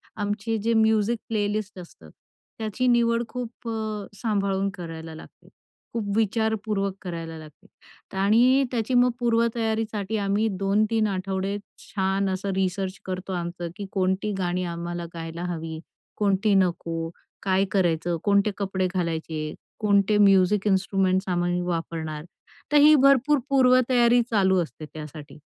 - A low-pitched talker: No, high, 195 Hz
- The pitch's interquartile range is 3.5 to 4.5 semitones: Yes, average, 3.8 semitones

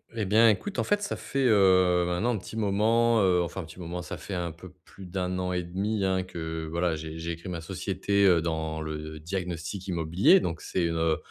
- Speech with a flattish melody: No, average, 3.1 semitones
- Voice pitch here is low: Yes, very low, 90 Hz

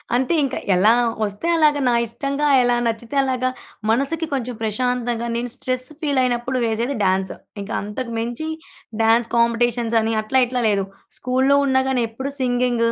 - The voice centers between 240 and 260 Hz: Yes, high, 245 Hz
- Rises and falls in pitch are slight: Yes, narrow, 2.3 semitones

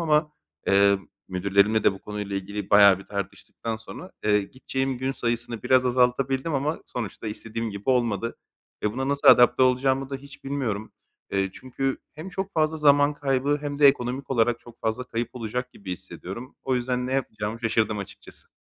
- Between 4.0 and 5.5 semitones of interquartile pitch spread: Yes, average, 4.3 semitones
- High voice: No, low, 125 Hz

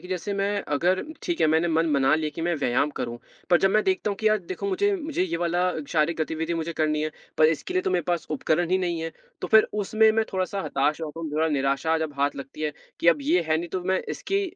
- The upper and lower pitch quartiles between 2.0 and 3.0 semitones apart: No, average, 3.4 semitones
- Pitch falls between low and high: Yes, medium, 170 Hz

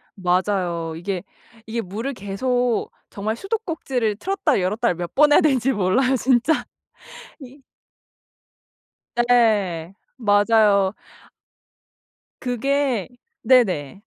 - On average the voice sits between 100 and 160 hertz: No, high, 225 Hz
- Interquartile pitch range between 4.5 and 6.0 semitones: Yes, average, 5.1 semitones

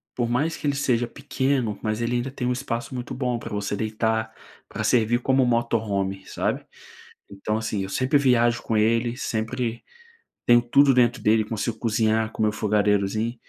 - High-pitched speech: No, low, 115 Hz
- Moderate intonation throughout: No, narrow, 2.3 semitones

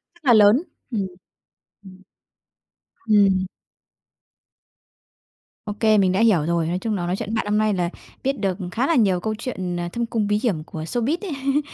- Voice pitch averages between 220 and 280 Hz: No, high, 210 Hz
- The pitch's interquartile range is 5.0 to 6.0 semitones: No, average, 4.2 semitones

